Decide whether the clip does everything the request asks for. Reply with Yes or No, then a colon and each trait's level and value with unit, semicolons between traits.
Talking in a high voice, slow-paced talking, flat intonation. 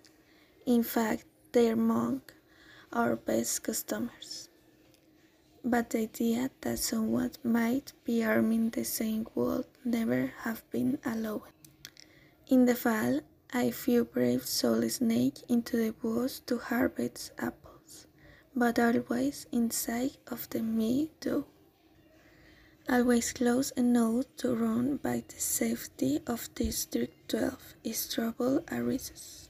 Yes: high, 240 Hz; slow, 115 wpm; narrow, 2.1 semitones